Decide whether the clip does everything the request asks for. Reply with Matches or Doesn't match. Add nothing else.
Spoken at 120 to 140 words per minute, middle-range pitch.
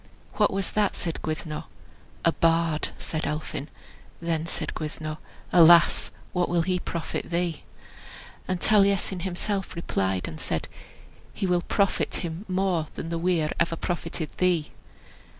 Matches